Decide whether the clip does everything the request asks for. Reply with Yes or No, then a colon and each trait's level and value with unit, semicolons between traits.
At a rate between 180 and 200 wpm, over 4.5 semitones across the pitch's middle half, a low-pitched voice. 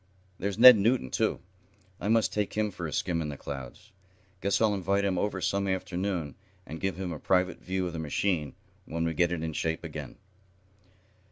No: average, 195 wpm; average, 3.6 semitones; very low, 95 Hz